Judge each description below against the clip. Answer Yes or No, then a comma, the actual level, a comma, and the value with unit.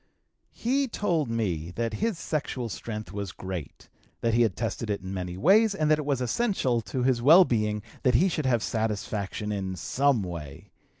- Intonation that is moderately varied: No, wide, 6.6 semitones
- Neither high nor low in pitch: No, low, 115 Hz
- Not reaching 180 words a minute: No, average, 185 wpm